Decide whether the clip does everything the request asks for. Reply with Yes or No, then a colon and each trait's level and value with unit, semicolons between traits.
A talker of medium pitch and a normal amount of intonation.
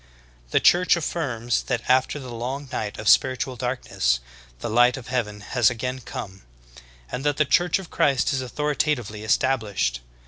No: low, 125 Hz; average, 3.5 semitones